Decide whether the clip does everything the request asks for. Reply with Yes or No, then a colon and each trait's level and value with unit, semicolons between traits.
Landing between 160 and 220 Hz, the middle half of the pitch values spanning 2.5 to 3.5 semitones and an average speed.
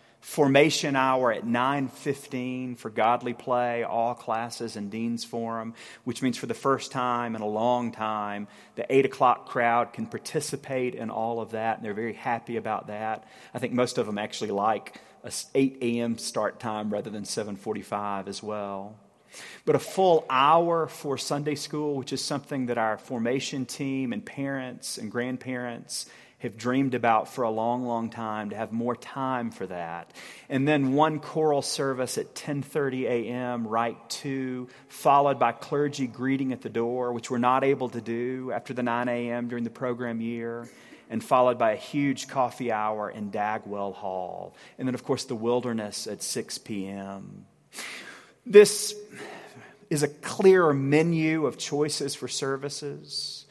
No: low, 125 Hz; average, 3.0 semitones; average, 165 wpm